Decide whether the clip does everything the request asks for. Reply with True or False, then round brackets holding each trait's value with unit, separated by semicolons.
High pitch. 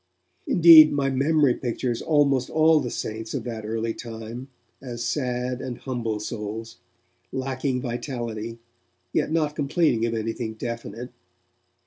False (125 Hz)